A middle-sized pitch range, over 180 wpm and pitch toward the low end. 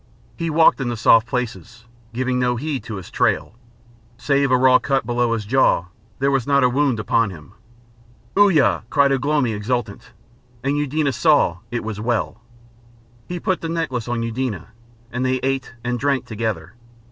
No: average, 3.6 semitones; average, 170 wpm; low, 125 Hz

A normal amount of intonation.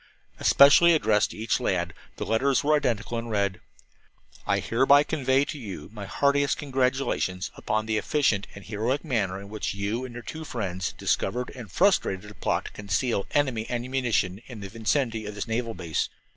Yes: average, 4.7 semitones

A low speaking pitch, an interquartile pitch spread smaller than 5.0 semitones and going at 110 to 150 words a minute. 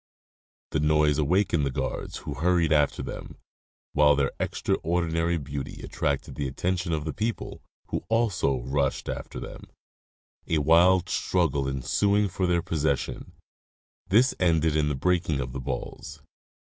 Yes: very low, 80 Hz; average, 3.9 semitones; average, 140 wpm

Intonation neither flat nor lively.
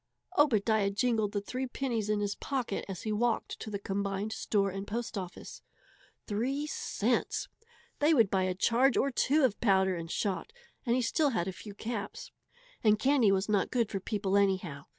Yes: average, 3.6 semitones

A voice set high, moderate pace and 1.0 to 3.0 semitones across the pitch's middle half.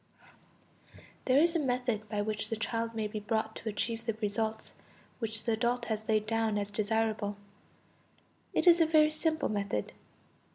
Yes: high, 220 Hz; average, 165 wpm; narrow, 2.4 semitones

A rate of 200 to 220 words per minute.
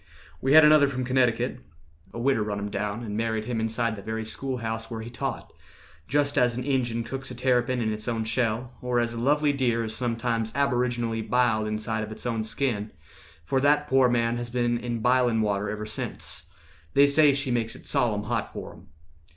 Yes: fast, 205 wpm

